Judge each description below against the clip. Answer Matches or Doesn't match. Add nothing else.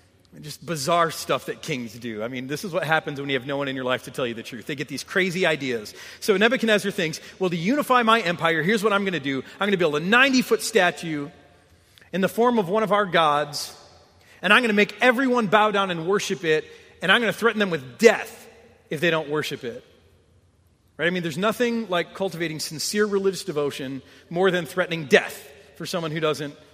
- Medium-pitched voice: Matches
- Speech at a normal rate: Doesn't match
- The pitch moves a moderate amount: Doesn't match